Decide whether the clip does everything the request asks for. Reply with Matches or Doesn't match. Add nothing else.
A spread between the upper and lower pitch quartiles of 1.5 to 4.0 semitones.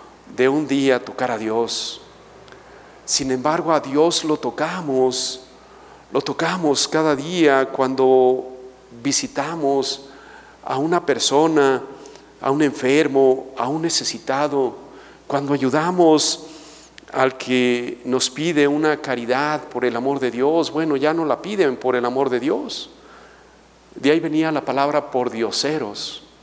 Matches